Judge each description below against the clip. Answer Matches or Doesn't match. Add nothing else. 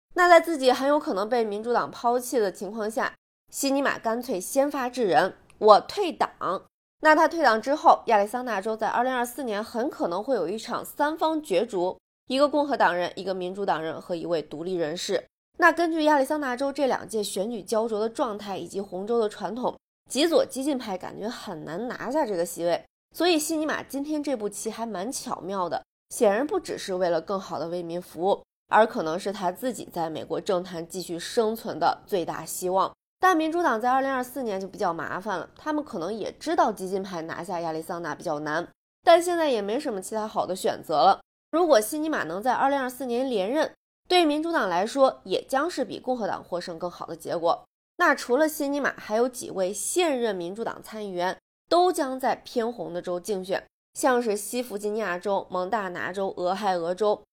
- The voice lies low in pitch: Doesn't match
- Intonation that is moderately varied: Doesn't match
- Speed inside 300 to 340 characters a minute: Matches